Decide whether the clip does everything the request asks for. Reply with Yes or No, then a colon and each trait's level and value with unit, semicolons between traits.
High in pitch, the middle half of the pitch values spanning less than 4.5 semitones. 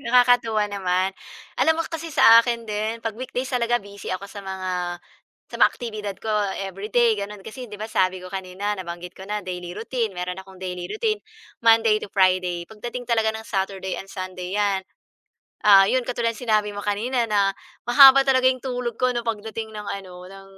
Yes: high, 210 Hz; average, 3.7 semitones